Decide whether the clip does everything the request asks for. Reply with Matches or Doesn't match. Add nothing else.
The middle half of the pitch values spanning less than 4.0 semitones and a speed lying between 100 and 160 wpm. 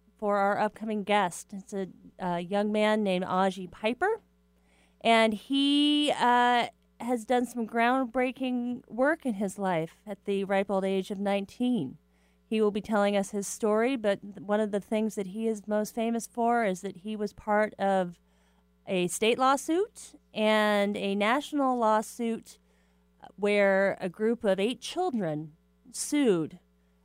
Matches